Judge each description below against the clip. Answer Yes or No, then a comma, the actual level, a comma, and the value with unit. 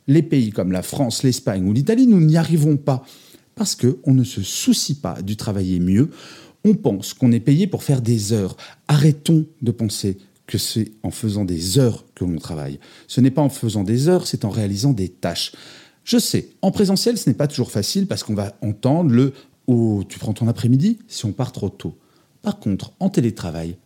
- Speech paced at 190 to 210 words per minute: Yes, average, 205 wpm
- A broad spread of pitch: Yes, wide, 6.6 semitones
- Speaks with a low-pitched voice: Yes, low, 125 Hz